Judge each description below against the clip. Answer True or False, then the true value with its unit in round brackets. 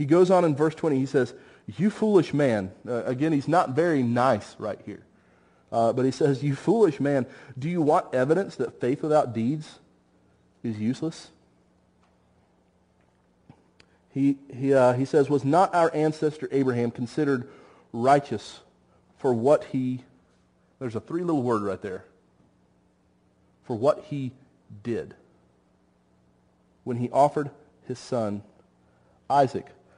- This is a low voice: True (125 Hz)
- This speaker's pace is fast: False (135 wpm)